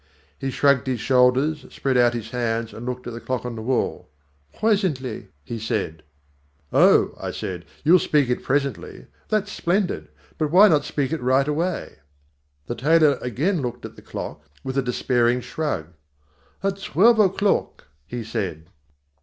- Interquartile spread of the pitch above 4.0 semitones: Yes, average, 5.0 semitones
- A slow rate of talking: No, average, 160 wpm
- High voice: No, low, 130 Hz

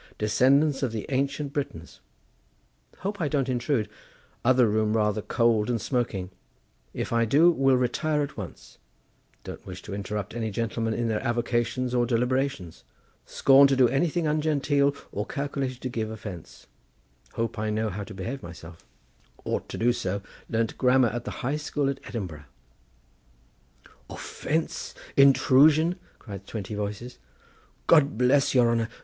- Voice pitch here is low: Yes, low, 120 Hz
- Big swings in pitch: No, average, 4.5 semitones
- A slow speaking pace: Yes, slow, 130 wpm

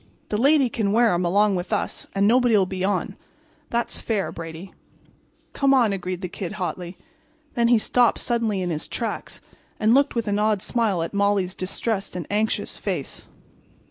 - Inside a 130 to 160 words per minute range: No, average, 175 wpm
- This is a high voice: Yes, high, 205 Hz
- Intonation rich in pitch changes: No, average, 3.9 semitones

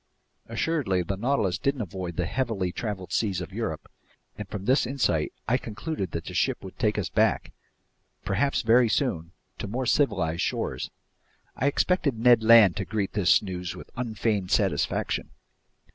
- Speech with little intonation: No, average, 5.3 semitones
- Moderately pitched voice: No, low, 105 Hz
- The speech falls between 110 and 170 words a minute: Yes, average, 150 wpm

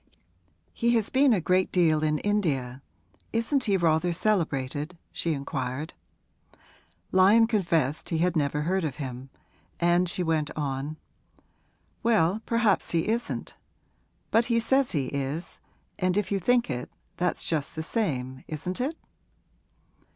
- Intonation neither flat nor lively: No, wide, 5.9 semitones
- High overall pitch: No, medium, 175 Hz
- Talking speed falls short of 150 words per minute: Yes, slow, 135 wpm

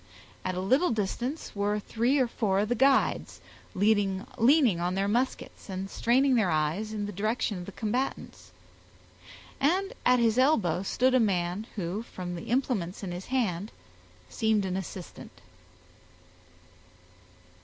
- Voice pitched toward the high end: Yes, high, 210 Hz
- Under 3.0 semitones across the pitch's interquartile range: No, average, 4.7 semitones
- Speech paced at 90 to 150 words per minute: Yes, average, 145 wpm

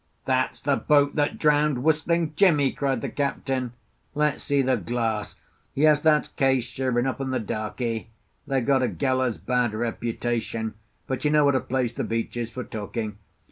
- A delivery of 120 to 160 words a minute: No, average, 175 wpm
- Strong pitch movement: No, average, 3.4 semitones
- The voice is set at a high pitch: No, low, 130 Hz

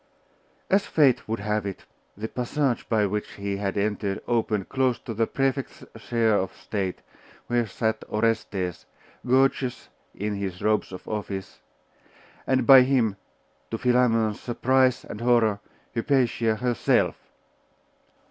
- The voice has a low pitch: Yes, low, 115 Hz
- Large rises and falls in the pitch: No, average, 3.4 semitones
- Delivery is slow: Yes, slow, 130 wpm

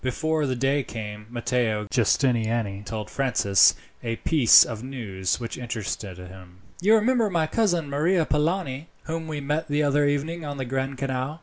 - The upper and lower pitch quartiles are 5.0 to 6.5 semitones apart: Yes, wide, 5.4 semitones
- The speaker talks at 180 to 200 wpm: No, average, 165 wpm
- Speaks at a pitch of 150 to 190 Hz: No, low, 135 Hz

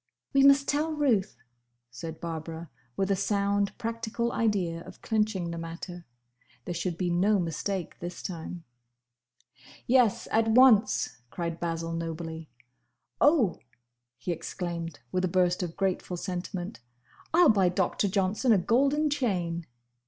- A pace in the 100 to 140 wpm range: Yes, slow, 135 wpm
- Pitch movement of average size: Yes, average, 4.7 semitones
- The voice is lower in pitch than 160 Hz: No, medium, 185 Hz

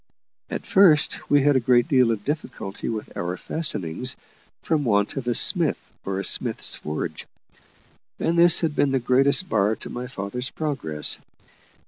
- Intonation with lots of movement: Yes, wide, 6.2 semitones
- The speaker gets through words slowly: No, average, 160 wpm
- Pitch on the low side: Yes, low, 125 Hz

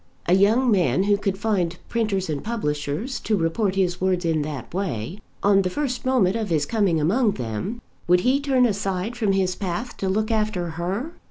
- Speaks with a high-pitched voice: Yes, high, 195 Hz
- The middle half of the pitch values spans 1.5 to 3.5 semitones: No, average, 4.2 semitones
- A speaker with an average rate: Yes, average, 190 wpm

